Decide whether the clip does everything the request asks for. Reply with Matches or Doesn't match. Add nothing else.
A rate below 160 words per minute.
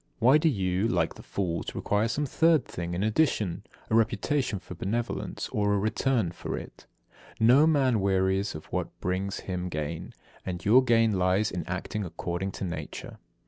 Doesn't match